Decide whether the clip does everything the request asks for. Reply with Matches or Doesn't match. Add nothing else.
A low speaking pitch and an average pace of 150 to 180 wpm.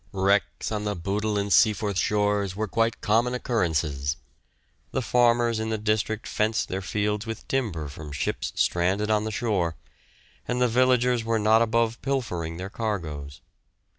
Matches